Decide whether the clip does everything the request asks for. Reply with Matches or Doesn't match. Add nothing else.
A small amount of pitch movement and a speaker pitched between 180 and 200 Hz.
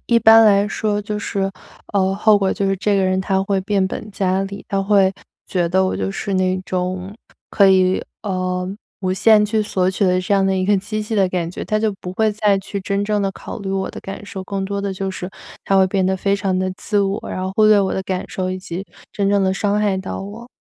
Matches